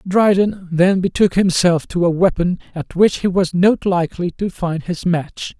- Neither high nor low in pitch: Yes, medium, 180 Hz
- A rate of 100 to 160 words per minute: No, average, 180 wpm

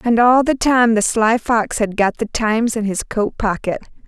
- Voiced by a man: No, female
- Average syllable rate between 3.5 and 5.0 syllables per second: Yes, 4.6 syllables/s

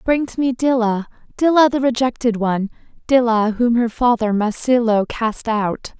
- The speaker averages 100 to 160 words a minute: Yes, average, 150 wpm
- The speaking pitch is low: No, high, 235 Hz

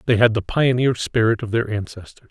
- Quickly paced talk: Yes, fast, 210 wpm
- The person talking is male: Yes, male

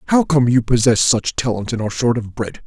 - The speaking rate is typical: No, fast, 245 wpm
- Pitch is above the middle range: No, low, 120 Hz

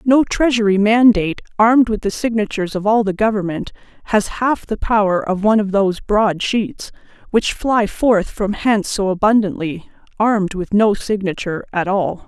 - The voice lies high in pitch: Yes, high, 210 Hz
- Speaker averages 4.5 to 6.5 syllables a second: Yes, 5.1 syllables/s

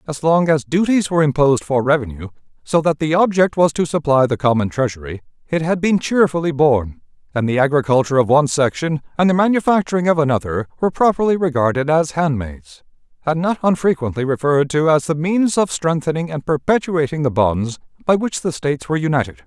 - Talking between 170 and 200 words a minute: Yes, average, 180 wpm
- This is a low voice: No, medium, 150 Hz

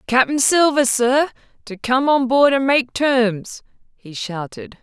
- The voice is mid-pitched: No, very high, 255 Hz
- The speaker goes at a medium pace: Yes, average, 150 wpm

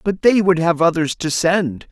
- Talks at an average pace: No, fast, 220 wpm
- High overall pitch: No, medium, 170 Hz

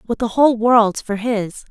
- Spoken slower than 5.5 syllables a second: Yes, 4.3 syllables/s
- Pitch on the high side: Yes, high, 225 Hz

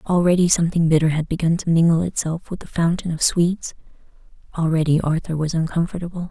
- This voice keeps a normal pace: Yes, average, 170 wpm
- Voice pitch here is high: No, medium, 165 Hz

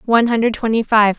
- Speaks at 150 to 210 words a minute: Yes, fast, 205 wpm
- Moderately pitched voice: No, high, 225 Hz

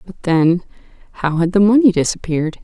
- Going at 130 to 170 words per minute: Yes, slow, 135 wpm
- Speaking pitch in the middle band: Yes, medium, 180 Hz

